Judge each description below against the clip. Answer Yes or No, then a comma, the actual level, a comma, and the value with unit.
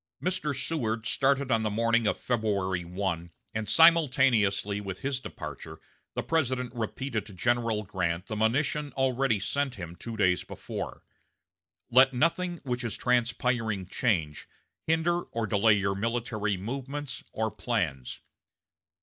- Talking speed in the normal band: No, slow, 130 wpm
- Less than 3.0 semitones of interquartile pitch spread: No, average, 4.7 semitones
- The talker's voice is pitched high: No, low, 115 Hz